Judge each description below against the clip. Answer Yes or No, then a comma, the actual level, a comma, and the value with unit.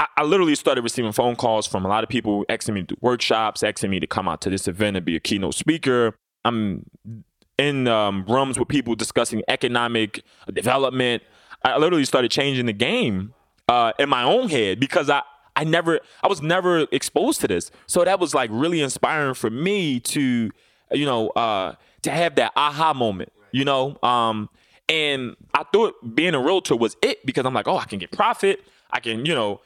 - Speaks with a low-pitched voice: Yes, low, 125 Hz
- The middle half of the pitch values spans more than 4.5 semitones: Yes, wide, 5.5 semitones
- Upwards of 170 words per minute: Yes, average, 200 wpm